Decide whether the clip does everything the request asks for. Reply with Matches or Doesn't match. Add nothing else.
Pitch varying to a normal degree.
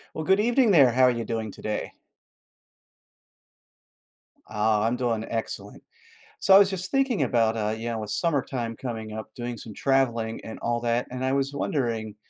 Matches